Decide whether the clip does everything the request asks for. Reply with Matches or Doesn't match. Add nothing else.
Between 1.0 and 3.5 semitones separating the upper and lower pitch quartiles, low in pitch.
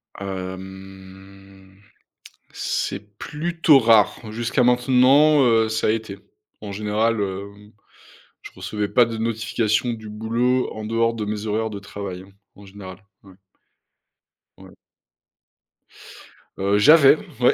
Matches